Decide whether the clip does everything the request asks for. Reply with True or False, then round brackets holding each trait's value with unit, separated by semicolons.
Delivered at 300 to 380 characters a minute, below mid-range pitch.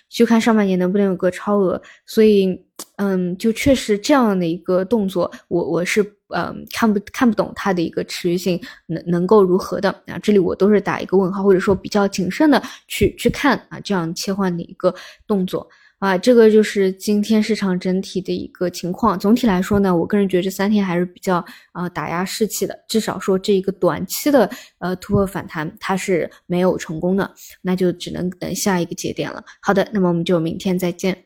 False (310 characters per minute; 190 Hz)